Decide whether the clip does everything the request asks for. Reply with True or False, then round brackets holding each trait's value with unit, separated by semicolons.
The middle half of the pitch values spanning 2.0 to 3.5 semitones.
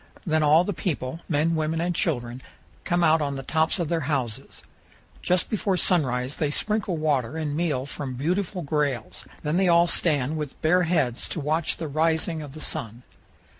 True (3.2 semitones)